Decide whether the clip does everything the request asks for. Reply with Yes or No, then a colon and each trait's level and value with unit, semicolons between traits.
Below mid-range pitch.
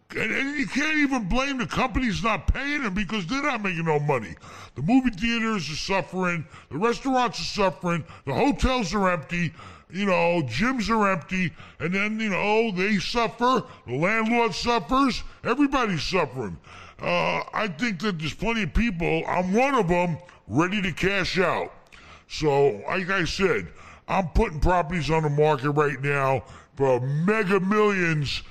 No: high, 190 Hz